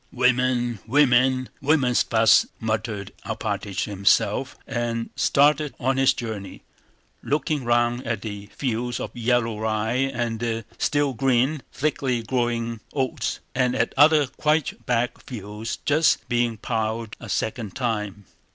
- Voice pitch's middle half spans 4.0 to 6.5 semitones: No, average, 2.8 semitones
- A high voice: No, low, 120 Hz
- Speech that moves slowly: Yes, slow, 130 wpm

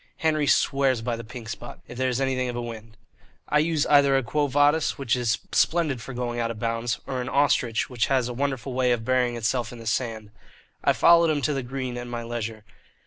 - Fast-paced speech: Yes, fast, 230 wpm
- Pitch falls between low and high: No, low, 125 Hz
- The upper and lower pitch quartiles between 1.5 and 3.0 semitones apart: Yes, average, 2.7 semitones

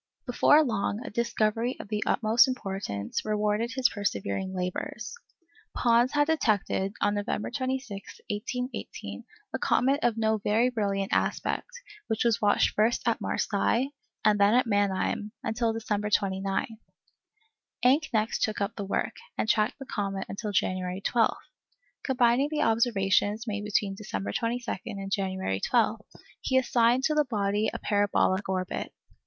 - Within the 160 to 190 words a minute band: No, average, 145 wpm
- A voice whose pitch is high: Yes, high, 215 Hz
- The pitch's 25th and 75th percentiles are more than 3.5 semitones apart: No, average, 3.2 semitones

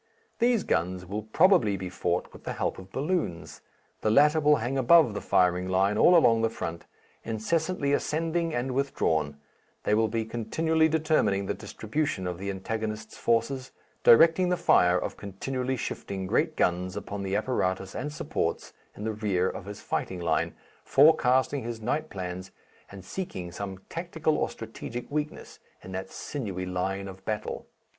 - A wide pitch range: Yes, wide, 7.7 semitones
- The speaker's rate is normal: Yes, average, 160 wpm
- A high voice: No, low, 110 Hz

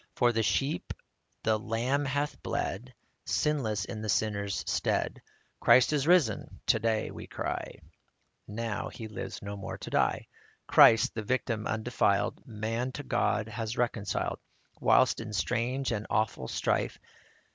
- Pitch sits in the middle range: No, low, 115 Hz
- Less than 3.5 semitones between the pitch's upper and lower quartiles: Yes, average, 3.0 semitones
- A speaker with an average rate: Yes, average, 145 wpm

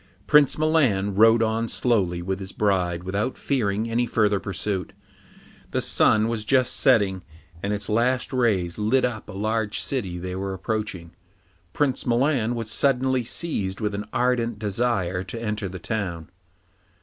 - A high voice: No, low, 110 Hz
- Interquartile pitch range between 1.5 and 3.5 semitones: No, average, 3.9 semitones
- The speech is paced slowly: No, average, 150 wpm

